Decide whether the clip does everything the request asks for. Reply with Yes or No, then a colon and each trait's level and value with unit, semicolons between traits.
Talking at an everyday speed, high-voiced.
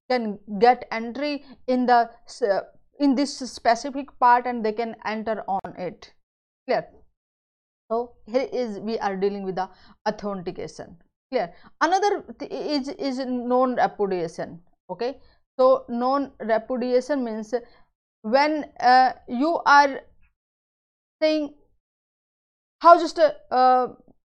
No: slow, 120 wpm; high, 245 Hz